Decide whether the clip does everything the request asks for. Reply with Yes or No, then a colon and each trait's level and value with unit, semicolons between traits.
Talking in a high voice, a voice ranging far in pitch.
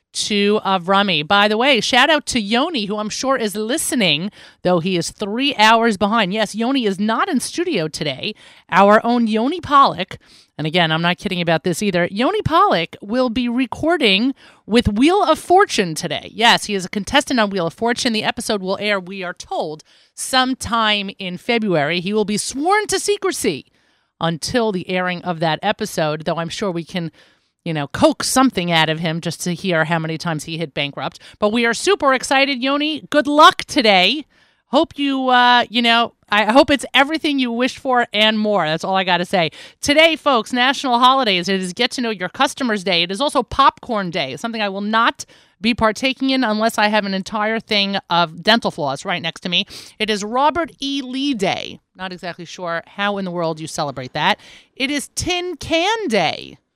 Yes: high, 215 Hz; wide, 6.3 semitones